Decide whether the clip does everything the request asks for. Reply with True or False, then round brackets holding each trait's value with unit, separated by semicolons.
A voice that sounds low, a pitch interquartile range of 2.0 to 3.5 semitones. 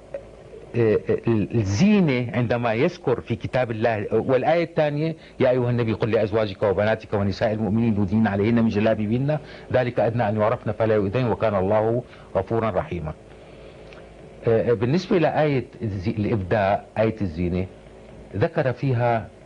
True (115 Hz; 2.9 semitones)